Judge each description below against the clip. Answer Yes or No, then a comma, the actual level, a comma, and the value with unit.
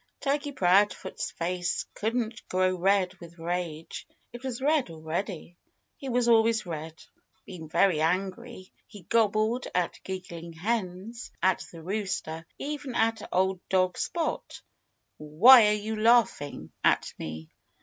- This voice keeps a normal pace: No, slow, 130 wpm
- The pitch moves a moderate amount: Yes, average, 5.0 semitones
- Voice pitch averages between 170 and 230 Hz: Yes, high, 190 Hz